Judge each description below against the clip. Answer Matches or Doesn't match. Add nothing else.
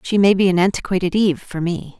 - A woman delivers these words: Matches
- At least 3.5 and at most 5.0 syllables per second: Doesn't match